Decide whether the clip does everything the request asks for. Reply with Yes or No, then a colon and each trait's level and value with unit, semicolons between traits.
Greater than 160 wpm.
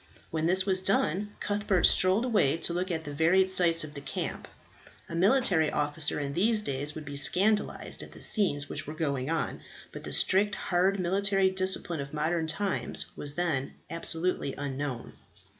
Yes: average, 175 wpm